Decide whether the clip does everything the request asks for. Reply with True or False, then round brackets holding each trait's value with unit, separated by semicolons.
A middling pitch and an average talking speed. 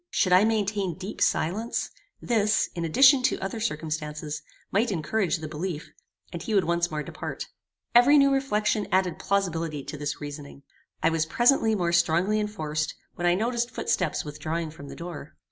True (175 Hz; 165 wpm)